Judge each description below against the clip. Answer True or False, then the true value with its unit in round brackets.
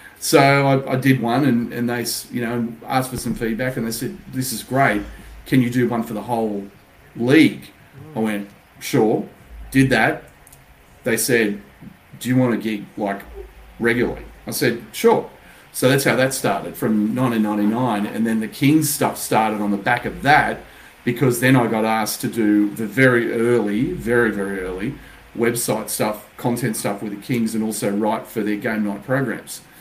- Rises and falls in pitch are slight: False (3.3 semitones)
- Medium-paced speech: True (185 wpm)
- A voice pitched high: False (115 Hz)